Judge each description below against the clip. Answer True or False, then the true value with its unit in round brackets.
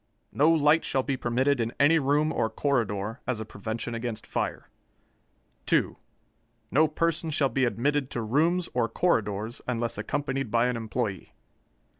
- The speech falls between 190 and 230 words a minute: False (150 wpm)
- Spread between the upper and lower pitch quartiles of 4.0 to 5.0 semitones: True (4.3 semitones)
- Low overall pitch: True (125 Hz)